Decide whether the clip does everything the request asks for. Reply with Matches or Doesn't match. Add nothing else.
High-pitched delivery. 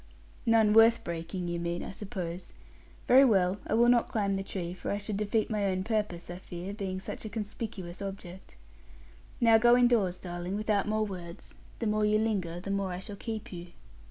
Matches